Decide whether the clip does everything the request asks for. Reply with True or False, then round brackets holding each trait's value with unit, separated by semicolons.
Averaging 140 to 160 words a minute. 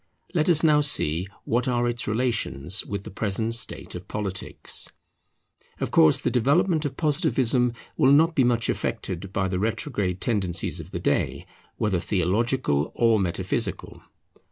True (150 wpm)